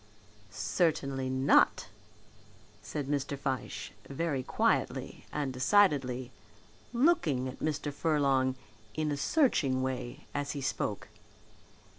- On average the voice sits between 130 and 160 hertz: Yes, medium, 140 Hz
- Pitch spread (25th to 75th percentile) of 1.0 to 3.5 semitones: Yes, narrow, 2.6 semitones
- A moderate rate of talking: No, slow, 100 wpm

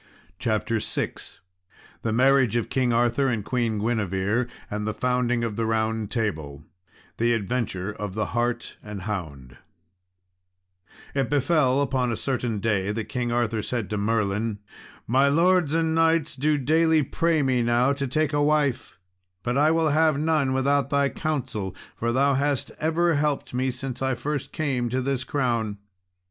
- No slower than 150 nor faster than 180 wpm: Yes, average, 160 wpm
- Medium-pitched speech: No, low, 125 Hz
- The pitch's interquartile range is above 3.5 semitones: Yes, average, 4.2 semitones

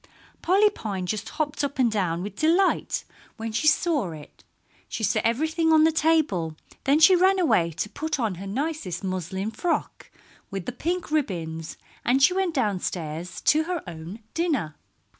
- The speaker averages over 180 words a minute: No, average, 165 wpm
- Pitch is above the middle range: Yes, high, 240 Hz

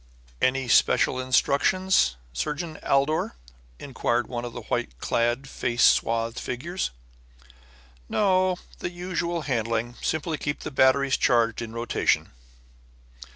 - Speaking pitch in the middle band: No, low, 130 Hz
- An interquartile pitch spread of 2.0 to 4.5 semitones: No, average, 5.3 semitones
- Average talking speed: No, slow, 110 wpm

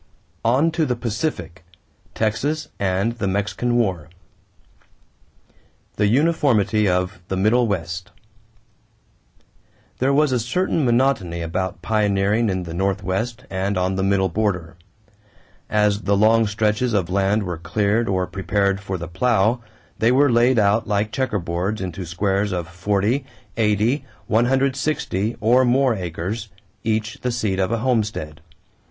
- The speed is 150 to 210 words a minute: No, slow, 135 wpm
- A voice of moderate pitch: No, low, 105 Hz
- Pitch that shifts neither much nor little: Yes, average, 4.1 semitones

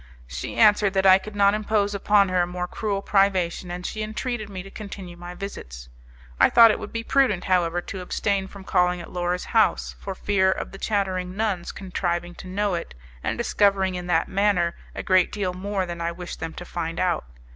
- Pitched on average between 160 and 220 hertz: Yes, high, 190 Hz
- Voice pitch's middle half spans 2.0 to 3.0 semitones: Yes, narrow, 2.4 semitones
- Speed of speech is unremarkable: No, fast, 210 wpm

